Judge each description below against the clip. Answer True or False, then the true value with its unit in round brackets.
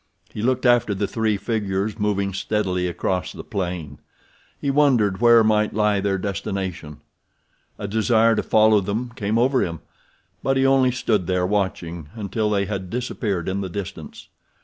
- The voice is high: False (105 Hz)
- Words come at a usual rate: True (160 wpm)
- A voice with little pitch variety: False (3.0 semitones)